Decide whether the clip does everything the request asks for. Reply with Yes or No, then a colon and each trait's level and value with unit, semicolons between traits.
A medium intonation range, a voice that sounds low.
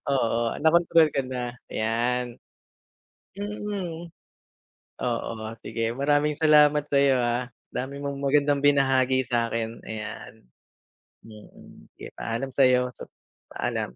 Yes: average, 3.6 semitones; low, 130 Hz